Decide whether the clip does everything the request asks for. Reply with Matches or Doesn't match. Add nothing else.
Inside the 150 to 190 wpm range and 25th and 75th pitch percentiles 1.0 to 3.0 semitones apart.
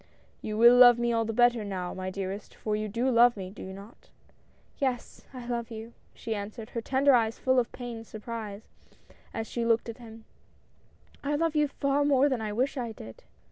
Doesn't match